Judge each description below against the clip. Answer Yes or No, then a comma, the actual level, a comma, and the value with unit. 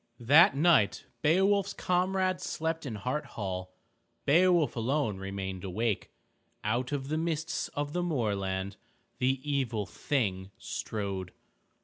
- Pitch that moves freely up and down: Yes, wide, 8.3 semitones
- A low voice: Yes, low, 130 Hz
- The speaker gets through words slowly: Yes, slow, 115 wpm